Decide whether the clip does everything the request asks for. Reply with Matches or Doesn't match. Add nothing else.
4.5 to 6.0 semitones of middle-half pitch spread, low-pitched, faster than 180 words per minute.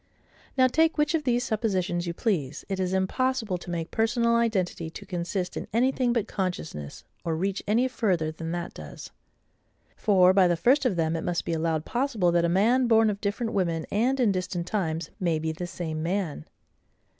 Doesn't match